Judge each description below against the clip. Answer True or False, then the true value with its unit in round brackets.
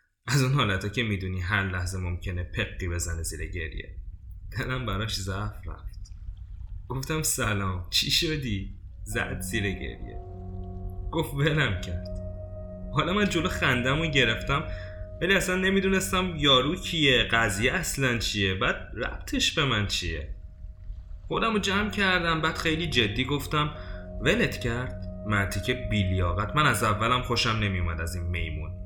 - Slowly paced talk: False (135 wpm)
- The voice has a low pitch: True (100 Hz)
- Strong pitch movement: True (6.6 semitones)